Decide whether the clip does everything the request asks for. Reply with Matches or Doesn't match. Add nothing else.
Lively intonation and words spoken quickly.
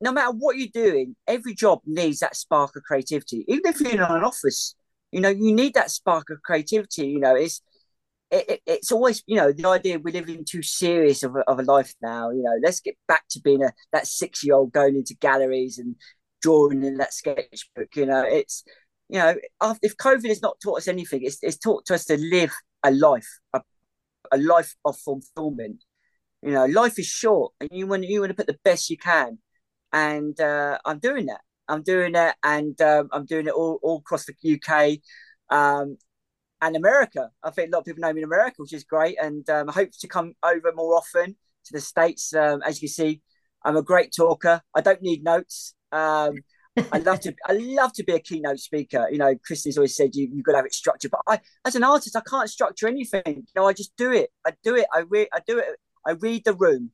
Matches